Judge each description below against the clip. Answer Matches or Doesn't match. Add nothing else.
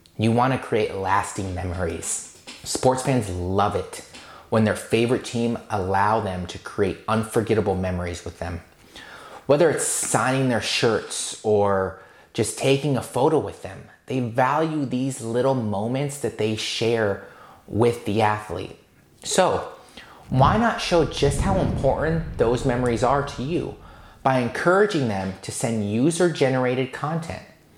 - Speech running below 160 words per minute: Matches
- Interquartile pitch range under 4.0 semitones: Doesn't match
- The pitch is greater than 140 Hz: Doesn't match